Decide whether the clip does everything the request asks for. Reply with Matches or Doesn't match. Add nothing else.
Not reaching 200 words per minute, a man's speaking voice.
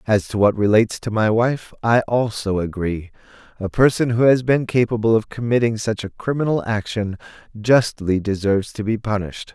Matches